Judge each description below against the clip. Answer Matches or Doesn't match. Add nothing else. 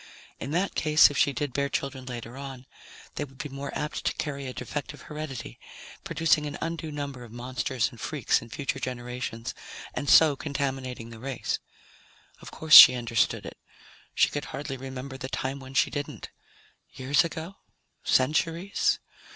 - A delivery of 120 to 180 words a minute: Matches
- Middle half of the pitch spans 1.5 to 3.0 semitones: Matches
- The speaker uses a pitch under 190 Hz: Matches